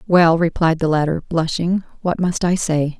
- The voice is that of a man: No, female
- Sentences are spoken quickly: No, average, 180 wpm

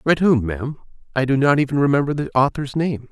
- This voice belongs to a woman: No, male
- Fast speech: No, average, 190 wpm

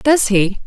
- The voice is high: Yes, high, 235 Hz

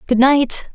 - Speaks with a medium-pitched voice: No, very high, 260 Hz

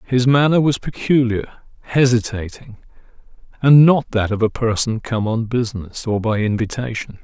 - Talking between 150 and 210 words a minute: No, average, 140 wpm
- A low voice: Yes, low, 115 Hz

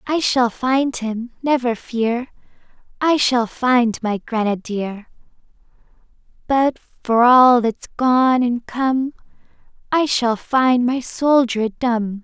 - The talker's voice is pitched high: Yes, high, 245 Hz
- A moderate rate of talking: No, slow, 120 wpm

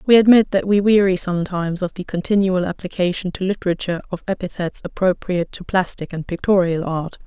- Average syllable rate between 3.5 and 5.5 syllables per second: No, 6.1 syllables/s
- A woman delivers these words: Yes, female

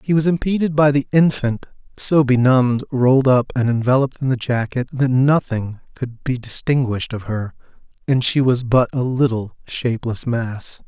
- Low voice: Yes, low, 130 Hz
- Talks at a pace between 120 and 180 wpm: Yes, average, 165 wpm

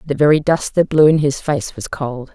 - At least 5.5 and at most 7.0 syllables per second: No, 5.1 syllables/s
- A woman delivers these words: Yes, female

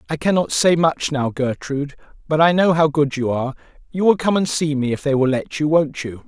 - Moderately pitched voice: Yes, medium, 150 Hz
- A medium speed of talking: No, fast, 250 wpm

